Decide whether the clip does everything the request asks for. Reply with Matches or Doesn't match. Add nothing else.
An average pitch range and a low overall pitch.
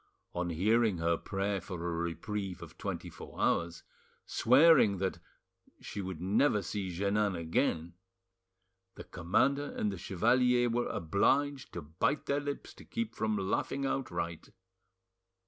Doesn't match